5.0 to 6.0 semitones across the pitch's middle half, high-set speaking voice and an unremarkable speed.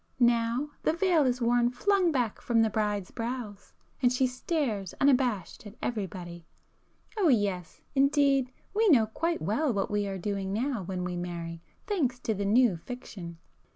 Yes: average, 5.3 semitones; high, 235 Hz; average, 155 wpm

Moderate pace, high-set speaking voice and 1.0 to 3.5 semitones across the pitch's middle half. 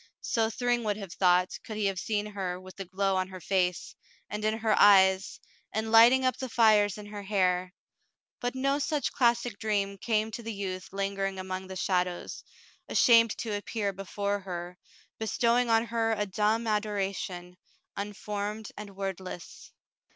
Yes: average, 165 wpm; high, 205 Hz; average, 2.8 semitones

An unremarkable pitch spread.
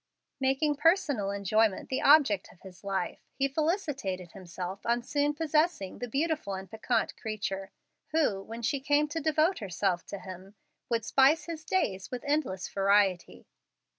No: wide, 7.4 semitones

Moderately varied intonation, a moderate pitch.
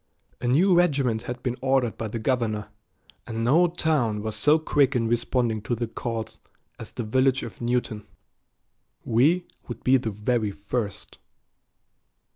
No: average, 3.1 semitones; low, 120 Hz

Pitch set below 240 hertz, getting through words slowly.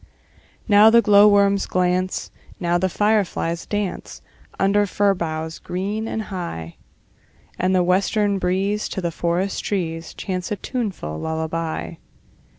Yes: medium, 185 Hz; slow, 125 wpm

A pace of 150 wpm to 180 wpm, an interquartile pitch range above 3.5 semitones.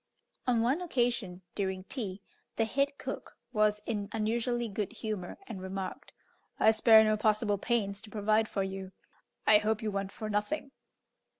No: average, 160 wpm; narrow, 2.4 semitones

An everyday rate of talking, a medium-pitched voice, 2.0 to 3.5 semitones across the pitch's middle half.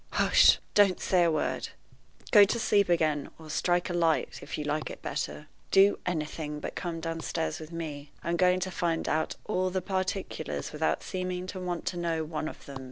Yes: average, 195 wpm; medium, 170 Hz; average, 2.8 semitones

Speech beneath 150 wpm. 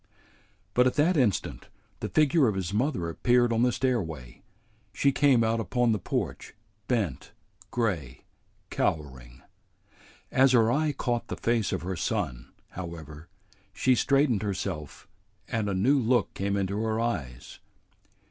Yes: average, 140 wpm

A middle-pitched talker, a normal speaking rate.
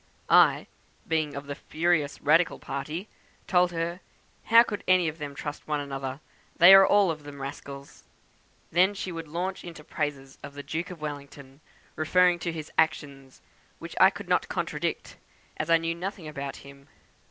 Yes: medium, 155 Hz; average, 175 wpm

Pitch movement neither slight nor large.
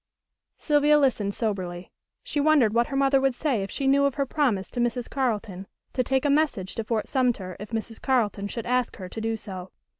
Yes: average, 4.9 semitones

